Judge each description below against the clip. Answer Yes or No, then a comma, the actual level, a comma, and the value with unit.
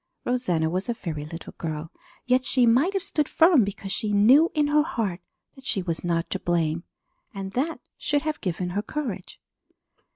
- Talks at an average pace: Yes, average, 185 wpm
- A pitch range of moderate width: No, wide, 8.2 semitones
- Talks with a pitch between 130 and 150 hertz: No, high, 205 Hz